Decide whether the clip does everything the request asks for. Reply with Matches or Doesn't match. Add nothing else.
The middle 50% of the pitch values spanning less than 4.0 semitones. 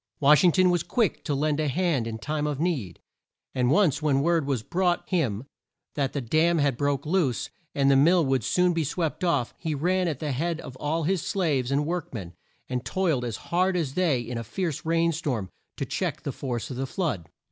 Doesn't match